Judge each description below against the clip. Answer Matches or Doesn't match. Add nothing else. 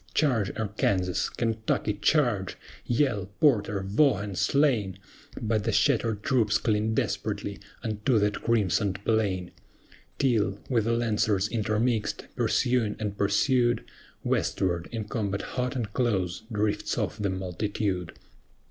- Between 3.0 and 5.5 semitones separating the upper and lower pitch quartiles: Doesn't match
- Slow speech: Matches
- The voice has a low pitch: Matches